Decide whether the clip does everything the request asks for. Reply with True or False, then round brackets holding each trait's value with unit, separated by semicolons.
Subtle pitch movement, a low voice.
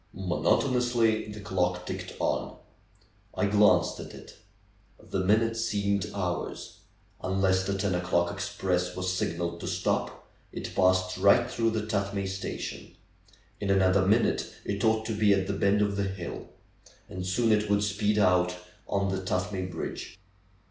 True (2.2 semitones; 100 Hz)